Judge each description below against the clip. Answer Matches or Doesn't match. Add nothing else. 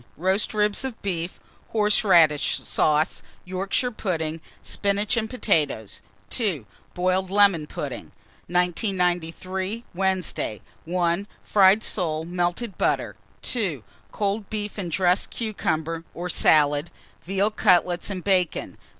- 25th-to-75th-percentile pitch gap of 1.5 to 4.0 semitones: Matches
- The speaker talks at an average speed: Doesn't match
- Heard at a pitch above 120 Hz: Matches